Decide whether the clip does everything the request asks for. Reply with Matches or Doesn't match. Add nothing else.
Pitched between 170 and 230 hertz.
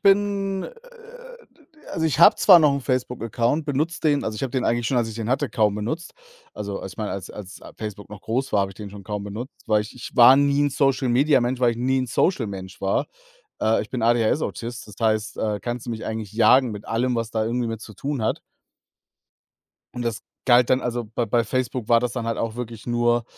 Doesn't match